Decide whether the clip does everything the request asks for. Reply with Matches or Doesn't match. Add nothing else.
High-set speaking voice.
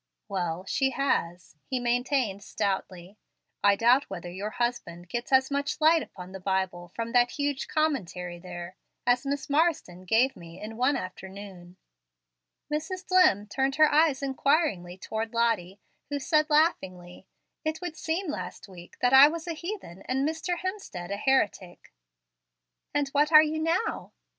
Matches